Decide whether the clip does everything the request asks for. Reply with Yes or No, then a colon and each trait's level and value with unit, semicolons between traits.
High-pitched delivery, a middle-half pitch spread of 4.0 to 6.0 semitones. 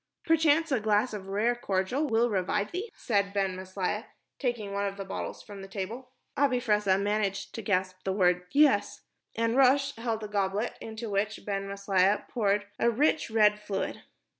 No: high, 210 Hz; average, 3.4 semitones